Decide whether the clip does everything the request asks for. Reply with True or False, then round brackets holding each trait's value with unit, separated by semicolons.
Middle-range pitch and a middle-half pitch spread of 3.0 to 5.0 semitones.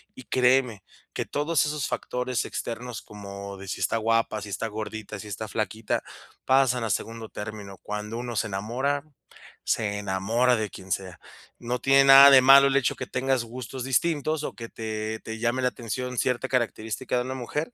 False (115 Hz; 3.3 semitones)